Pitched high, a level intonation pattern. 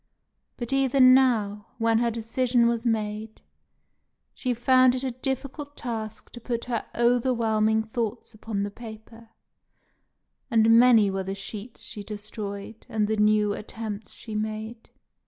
Yes: high, 225 Hz; narrow, 2.2 semitones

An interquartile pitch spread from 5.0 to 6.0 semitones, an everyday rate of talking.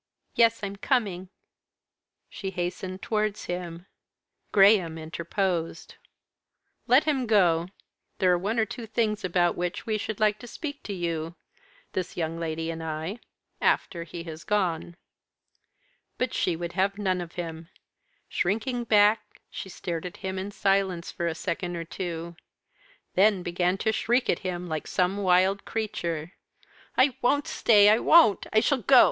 No: average, 3.8 semitones; average, 150 wpm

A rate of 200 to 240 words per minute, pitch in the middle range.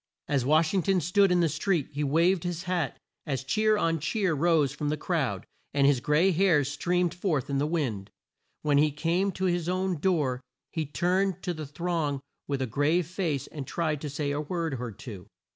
Yes: fast, 205 wpm; medium, 160 Hz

